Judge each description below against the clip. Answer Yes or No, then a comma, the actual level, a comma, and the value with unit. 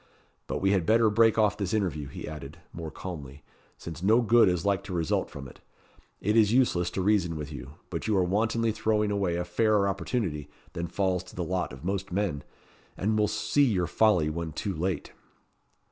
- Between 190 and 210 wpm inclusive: Yes, average, 200 wpm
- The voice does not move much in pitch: No, average, 4.2 semitones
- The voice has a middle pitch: No, very low, 95 Hz